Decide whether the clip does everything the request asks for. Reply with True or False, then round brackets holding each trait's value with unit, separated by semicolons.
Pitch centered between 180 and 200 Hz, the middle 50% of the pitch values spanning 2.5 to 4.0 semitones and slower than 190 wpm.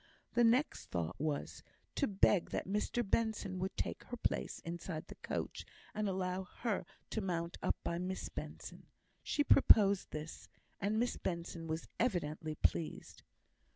False (185 Hz; 4.4 semitones; 150 wpm)